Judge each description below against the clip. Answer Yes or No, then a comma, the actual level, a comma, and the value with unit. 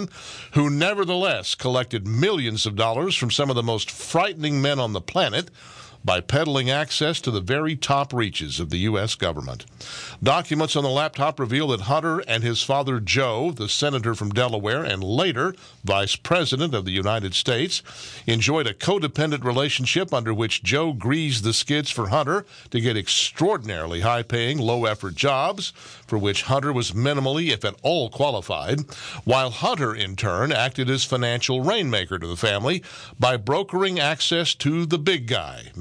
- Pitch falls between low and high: No, low, 130 Hz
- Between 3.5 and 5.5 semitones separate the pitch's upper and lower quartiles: Yes, average, 4.7 semitones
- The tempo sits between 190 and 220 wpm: No, average, 165 wpm